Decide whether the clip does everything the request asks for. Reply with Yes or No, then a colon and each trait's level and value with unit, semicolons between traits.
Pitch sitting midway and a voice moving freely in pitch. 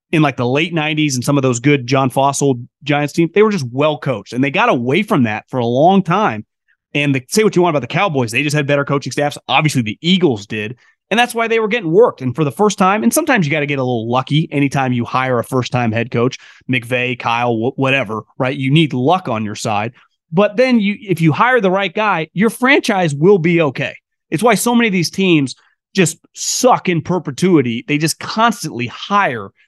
Yes: medium, 150 Hz; wide, 6.7 semitones